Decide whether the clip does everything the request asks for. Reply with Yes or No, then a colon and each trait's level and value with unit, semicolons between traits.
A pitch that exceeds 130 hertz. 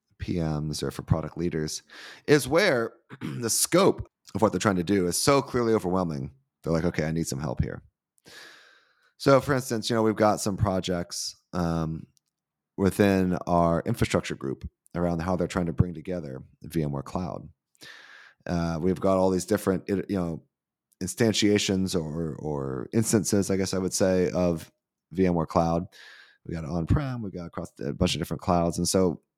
No: very low, 90 Hz